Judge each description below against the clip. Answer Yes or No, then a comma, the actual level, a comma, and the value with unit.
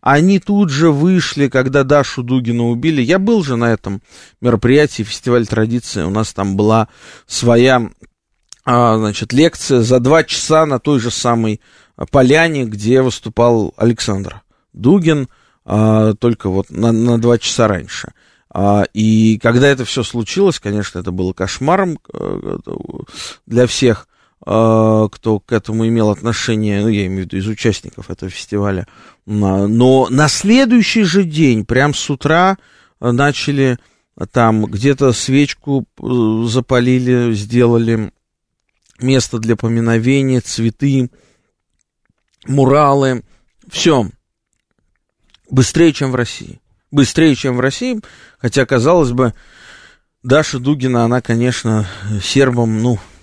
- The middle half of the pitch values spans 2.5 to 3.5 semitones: No, average, 4.0 semitones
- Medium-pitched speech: No, low, 120 Hz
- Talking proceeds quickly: No, average, 115 wpm